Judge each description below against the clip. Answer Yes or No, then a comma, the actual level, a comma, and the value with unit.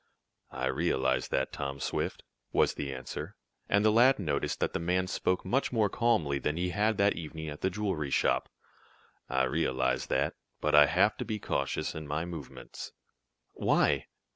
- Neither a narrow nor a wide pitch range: No, wide, 6.6 semitones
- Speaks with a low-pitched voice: Yes, very low, 80 Hz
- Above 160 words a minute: Yes, average, 170 wpm